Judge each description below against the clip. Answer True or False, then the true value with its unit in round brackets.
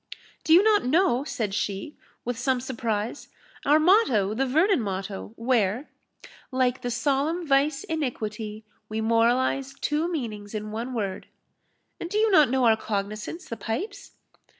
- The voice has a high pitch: True (250 Hz)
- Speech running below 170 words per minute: True (150 wpm)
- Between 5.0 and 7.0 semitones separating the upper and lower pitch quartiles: True (5.5 semitones)